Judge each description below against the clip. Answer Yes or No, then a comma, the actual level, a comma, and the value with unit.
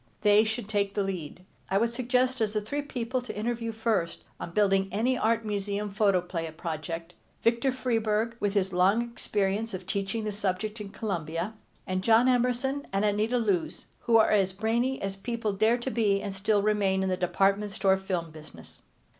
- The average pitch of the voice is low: No, high, 210 Hz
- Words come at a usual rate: Yes, average, 180 wpm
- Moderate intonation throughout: Yes, average, 3.1 semitones